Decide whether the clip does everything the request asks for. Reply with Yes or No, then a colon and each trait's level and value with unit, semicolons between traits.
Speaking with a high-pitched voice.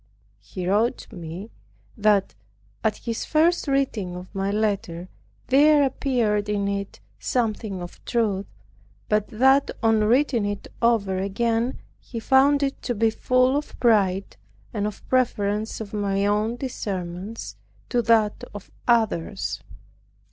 Yes: high, 215 Hz